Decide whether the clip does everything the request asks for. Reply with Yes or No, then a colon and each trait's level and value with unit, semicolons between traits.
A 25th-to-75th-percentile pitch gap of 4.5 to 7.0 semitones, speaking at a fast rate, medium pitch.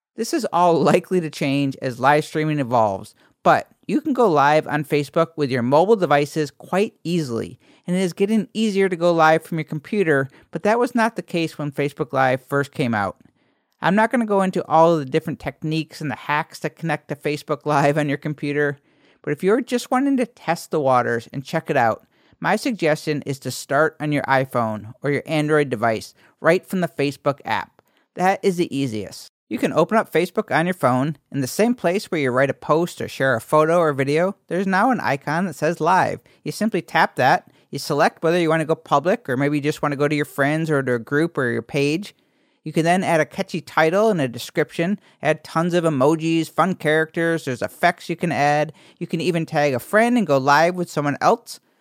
No: average, 3.7 semitones; fast, 225 wpm; medium, 155 Hz